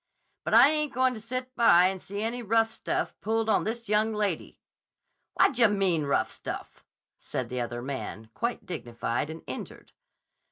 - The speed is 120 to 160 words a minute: No, average, 170 wpm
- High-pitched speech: Yes, high, 215 Hz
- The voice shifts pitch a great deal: Yes, wide, 6.5 semitones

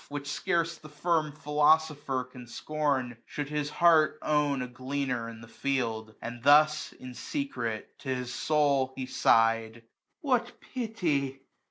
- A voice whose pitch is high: No, medium, 140 Hz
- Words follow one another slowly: No, average, 150 wpm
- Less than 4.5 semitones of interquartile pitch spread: Yes, average, 3.5 semitones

